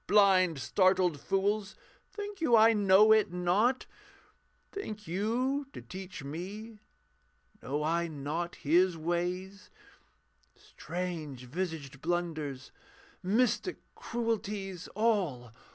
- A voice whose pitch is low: No, medium, 185 Hz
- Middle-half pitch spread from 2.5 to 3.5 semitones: No, average, 4.5 semitones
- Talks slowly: Yes, slow, 95 wpm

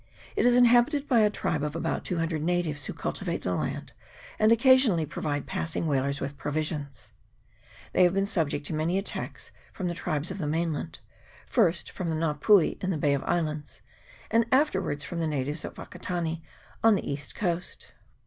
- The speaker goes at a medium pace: Yes, average, 185 wpm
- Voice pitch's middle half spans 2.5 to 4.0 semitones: No, average, 4.7 semitones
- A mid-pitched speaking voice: Yes, medium, 165 Hz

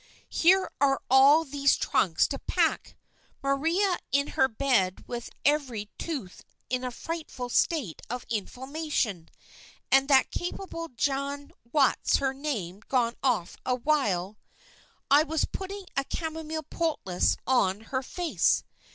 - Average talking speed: No, slow, 125 wpm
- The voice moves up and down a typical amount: Yes, average, 4.5 semitones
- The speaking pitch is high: Yes, very high, 275 Hz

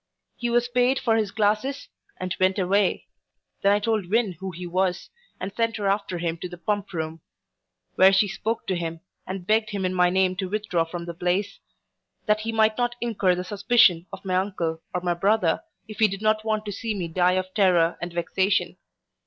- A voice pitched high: Yes, high, 195 Hz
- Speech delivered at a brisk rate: Yes, fast, 210 wpm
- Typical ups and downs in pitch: Yes, average, 3.2 semitones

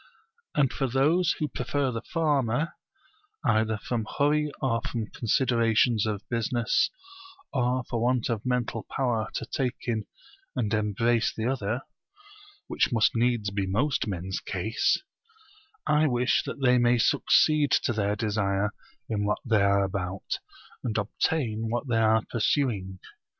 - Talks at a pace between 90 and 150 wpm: Yes, average, 140 wpm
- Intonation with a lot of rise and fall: No, average, 3.2 semitones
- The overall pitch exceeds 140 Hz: No, low, 115 Hz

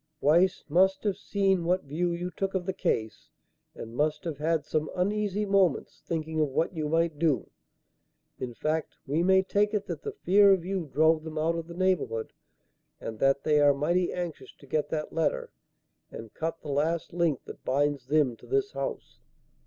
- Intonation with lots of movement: No, average, 3.9 semitones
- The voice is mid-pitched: Yes, medium, 165 Hz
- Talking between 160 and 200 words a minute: Yes, average, 190 wpm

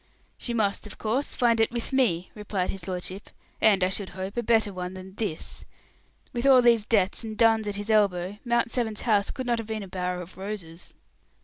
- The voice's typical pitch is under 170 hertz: No, high, 210 Hz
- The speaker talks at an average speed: No, fast, 210 wpm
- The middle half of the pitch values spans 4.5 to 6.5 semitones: No, average, 3.6 semitones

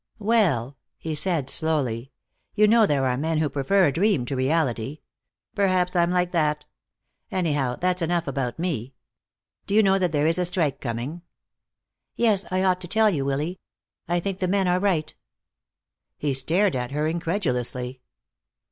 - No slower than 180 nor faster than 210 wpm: No, average, 165 wpm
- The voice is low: No, medium, 165 Hz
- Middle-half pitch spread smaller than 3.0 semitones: No, average, 5.2 semitones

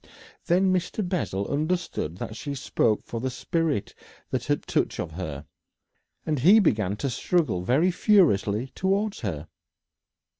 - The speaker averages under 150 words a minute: Yes, average, 140 wpm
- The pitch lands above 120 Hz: Yes, medium, 140 Hz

